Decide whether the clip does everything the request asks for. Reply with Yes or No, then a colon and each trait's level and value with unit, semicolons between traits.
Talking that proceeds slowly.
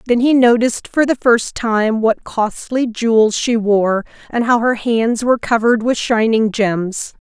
No: average, 175 wpm